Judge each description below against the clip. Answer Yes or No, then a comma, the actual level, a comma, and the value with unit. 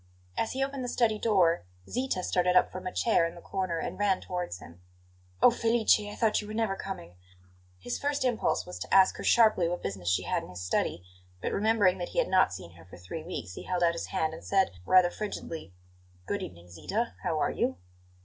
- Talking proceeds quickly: Yes, fast, 225 wpm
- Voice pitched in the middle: Yes, medium, 180 Hz